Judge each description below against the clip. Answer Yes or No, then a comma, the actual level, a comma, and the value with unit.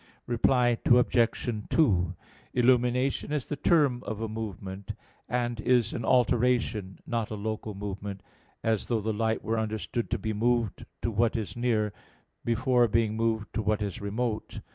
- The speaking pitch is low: Yes, low, 115 Hz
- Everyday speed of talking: Yes, average, 155 wpm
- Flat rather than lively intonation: Yes, narrow, 2.3 semitones